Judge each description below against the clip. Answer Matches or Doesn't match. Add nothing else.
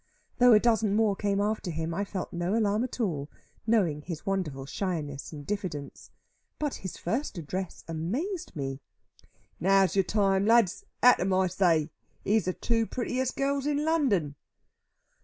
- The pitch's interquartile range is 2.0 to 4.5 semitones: Doesn't match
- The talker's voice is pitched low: Doesn't match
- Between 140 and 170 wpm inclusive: Matches